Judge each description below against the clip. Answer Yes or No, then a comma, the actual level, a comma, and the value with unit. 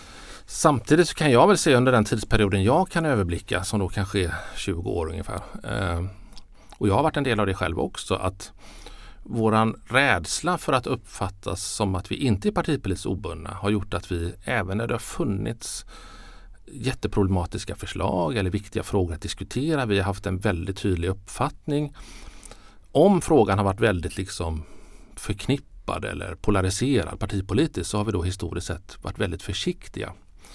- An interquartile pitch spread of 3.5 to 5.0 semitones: No, average, 3.0 semitones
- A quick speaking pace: No, average, 165 wpm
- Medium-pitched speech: No, low, 100 Hz